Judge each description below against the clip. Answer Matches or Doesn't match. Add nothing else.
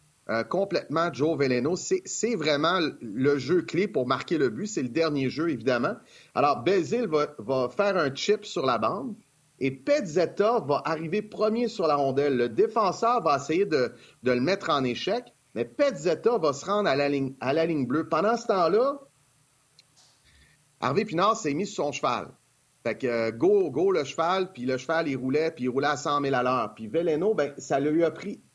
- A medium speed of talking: Matches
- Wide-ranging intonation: Matches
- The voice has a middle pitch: Matches